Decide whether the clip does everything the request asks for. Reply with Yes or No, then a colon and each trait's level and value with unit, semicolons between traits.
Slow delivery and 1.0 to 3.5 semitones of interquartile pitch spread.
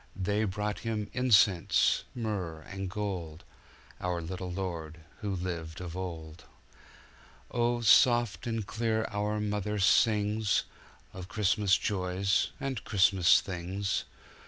Yes: slow, 110 wpm; average, 2.9 semitones